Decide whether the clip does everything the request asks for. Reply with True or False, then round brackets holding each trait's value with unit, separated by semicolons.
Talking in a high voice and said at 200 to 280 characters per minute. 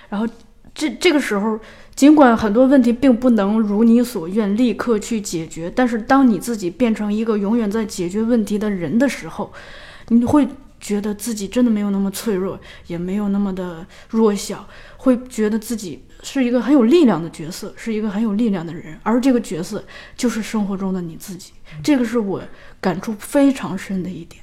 False (220 Hz; 290 characters per minute)